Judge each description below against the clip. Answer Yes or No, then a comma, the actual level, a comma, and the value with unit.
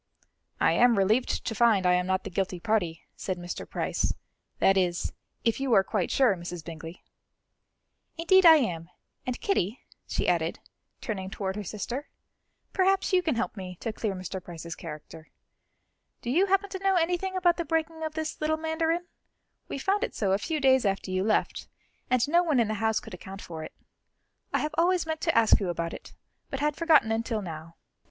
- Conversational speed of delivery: Yes, average, 195 wpm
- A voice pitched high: Yes, high, 225 Hz